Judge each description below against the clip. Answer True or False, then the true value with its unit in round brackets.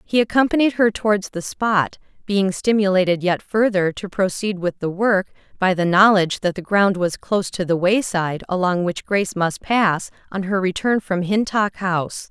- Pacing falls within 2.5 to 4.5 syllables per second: False (4.8 syllables/s)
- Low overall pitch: False (195 Hz)